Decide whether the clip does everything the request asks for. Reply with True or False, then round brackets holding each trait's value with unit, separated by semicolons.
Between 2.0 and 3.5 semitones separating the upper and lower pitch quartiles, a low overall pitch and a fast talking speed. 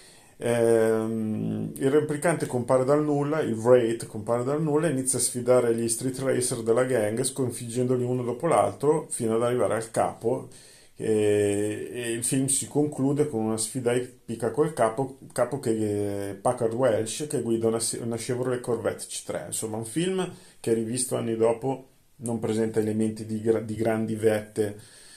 False (2.9 semitones; 120 Hz; 160 wpm)